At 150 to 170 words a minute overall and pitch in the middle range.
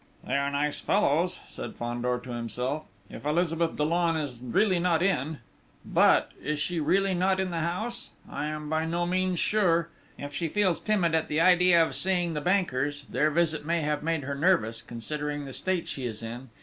No: average, 190 wpm; medium, 160 Hz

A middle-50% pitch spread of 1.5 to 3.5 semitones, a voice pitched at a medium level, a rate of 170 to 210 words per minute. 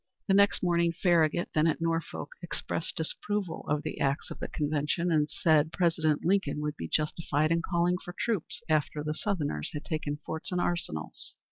Yes: average, 2.7 semitones; medium, 160 Hz; average, 175 wpm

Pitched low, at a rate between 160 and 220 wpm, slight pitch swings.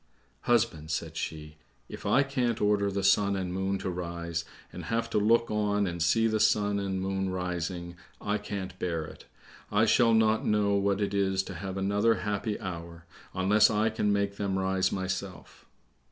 Yes: low, 100 Hz; average, 180 wpm; narrow, 2.2 semitones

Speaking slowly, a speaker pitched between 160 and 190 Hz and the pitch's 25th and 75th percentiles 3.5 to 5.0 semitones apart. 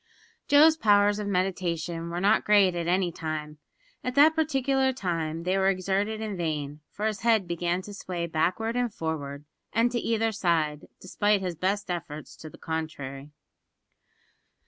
No: average, 160 wpm; medium, 185 Hz; average, 4.7 semitones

